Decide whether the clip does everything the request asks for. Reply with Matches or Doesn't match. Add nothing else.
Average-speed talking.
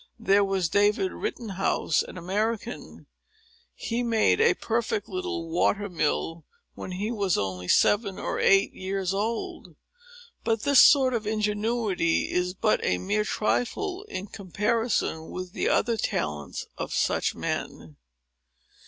Doesn't match